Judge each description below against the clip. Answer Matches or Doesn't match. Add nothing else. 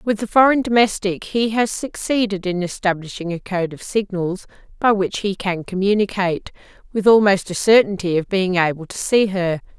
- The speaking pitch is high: Matches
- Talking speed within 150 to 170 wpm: Matches